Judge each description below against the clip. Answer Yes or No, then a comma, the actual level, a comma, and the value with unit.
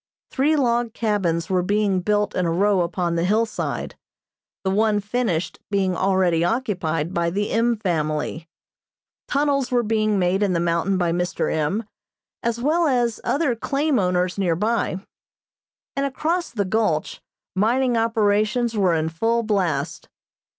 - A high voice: Yes, high, 205 Hz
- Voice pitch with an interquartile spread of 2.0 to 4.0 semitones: No, average, 4.7 semitones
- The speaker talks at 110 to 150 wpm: Yes, average, 145 wpm